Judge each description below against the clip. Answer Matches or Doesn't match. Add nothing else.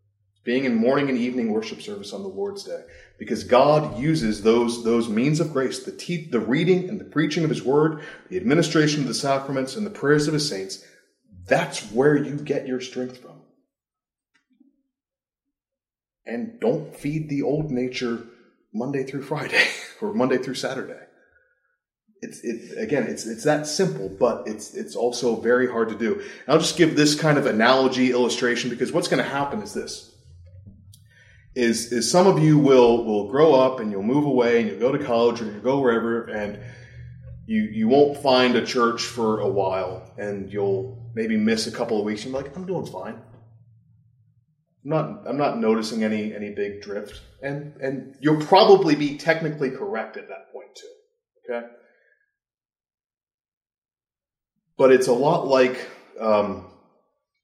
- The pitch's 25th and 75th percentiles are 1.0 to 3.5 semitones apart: Doesn't match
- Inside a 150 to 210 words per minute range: Matches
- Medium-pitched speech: Doesn't match